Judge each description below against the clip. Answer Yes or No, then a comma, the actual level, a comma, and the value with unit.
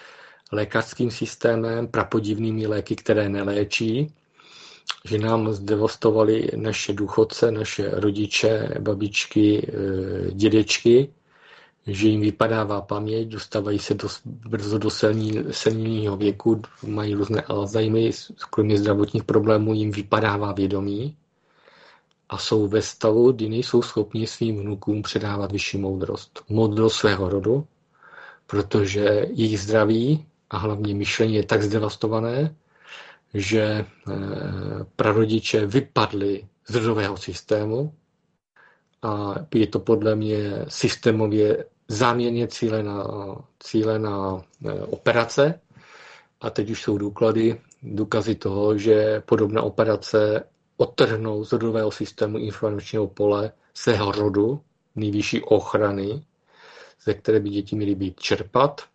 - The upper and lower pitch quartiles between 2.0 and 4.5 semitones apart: No, narrow, 1.5 semitones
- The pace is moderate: No, slow, 110 wpm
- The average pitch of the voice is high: No, low, 110 Hz